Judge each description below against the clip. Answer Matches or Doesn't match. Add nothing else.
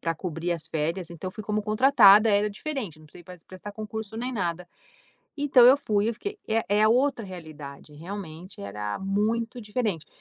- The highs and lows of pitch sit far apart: Doesn't match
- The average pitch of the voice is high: Matches